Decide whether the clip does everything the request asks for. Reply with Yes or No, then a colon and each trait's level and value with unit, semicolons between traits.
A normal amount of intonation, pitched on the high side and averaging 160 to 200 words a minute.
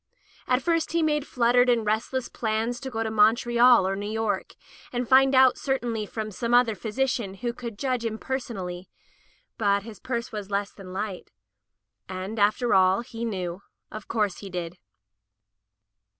Yes: average, 3.5 semitones; high, 225 Hz; average, 165 wpm